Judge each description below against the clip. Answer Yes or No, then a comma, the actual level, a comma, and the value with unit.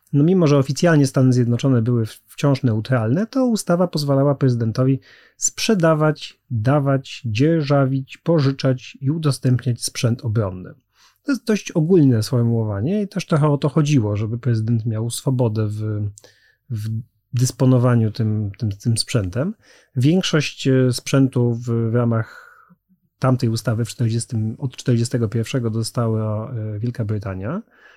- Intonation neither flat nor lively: Yes, average, 4.0 semitones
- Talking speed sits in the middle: Yes, average, 120 wpm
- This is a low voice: Yes, low, 125 Hz